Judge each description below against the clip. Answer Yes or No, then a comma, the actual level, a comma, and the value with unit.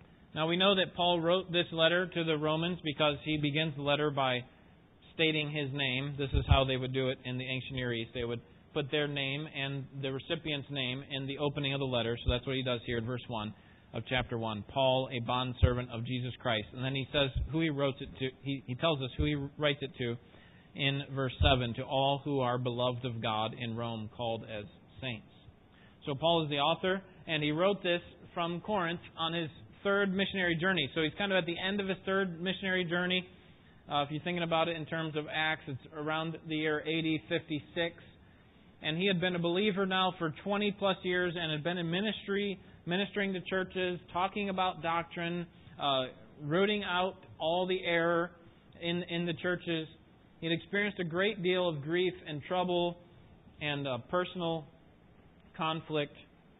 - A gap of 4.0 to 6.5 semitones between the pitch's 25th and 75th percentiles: Yes, average, 4.7 semitones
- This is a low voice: No, medium, 155 Hz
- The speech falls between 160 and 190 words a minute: No, average, 200 wpm